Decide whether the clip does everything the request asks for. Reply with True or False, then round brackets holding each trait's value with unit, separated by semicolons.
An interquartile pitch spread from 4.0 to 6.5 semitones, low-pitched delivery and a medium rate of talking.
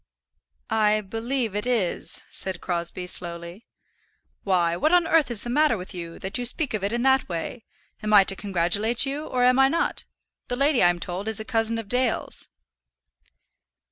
False (5.1 semitones; 220 Hz; 180 wpm)